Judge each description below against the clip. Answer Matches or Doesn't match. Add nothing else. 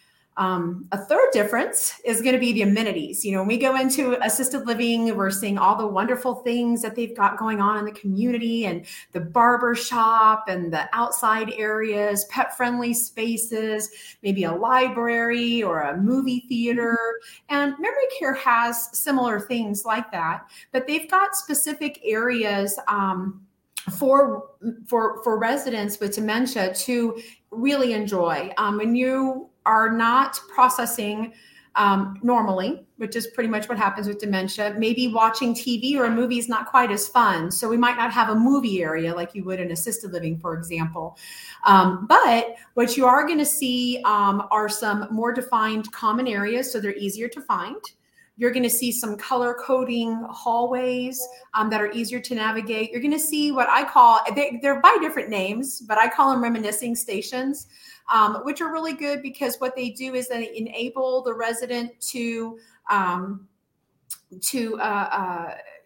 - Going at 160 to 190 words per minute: Matches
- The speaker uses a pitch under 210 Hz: Doesn't match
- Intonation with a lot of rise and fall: Doesn't match